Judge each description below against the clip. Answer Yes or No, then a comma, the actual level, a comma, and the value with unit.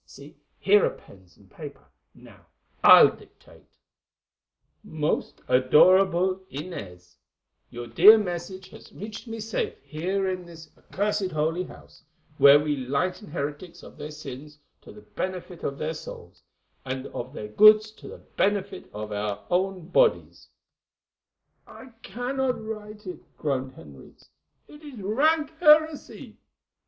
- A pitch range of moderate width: No, wide, 6.6 semitones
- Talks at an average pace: No, slow, 130 wpm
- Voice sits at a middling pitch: Yes, medium, 180 Hz